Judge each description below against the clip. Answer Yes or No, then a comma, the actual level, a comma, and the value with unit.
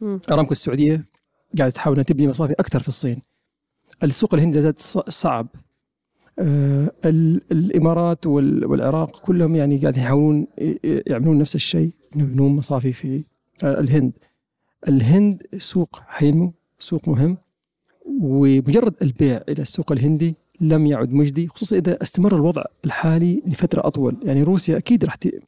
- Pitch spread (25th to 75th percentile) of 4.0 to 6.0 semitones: No, average, 3.3 semitones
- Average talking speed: Yes, average, 120 wpm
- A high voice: No, medium, 155 Hz